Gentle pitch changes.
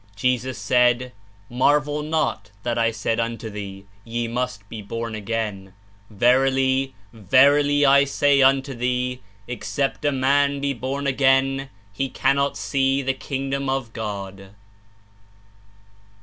No: average, 3.1 semitones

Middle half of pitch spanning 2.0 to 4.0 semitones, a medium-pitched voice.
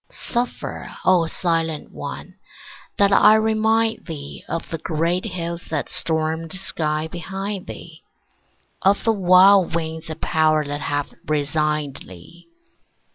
Yes: average, 3.6 semitones; medium, 165 Hz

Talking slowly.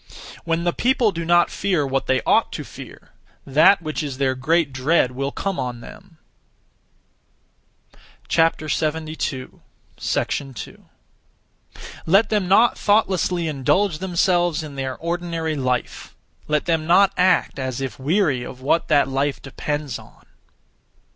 Yes: slow, 130 wpm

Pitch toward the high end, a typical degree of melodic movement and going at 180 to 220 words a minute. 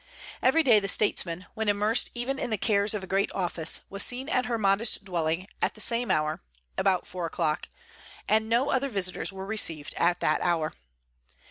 Yes: high, 200 Hz; average, 4.5 semitones; average, 190 wpm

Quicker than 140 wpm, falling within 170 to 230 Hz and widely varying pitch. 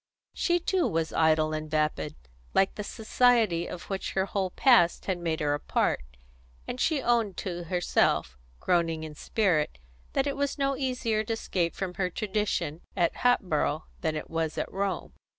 Yes: average, 170 wpm; medium, 185 Hz; wide, 5.9 semitones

